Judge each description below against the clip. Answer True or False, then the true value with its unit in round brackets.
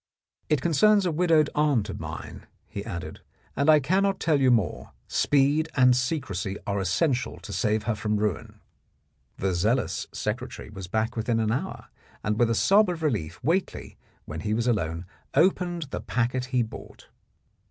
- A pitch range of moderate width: False (6.5 semitones)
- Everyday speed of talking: True (170 wpm)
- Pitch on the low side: True (125 Hz)